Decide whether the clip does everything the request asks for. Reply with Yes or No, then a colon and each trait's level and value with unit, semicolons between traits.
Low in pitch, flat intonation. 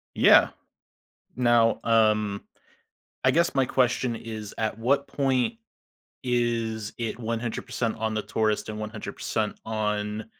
Yes: low, 115 Hz; narrow, 2.0 semitones